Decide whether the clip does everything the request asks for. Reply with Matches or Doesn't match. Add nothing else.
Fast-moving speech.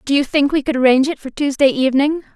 Matches